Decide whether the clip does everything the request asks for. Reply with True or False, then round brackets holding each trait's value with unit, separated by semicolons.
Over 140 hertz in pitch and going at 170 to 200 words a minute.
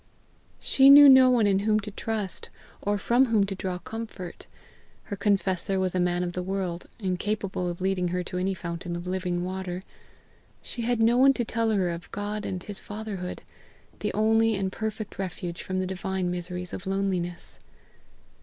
True (190 Hz; 180 wpm)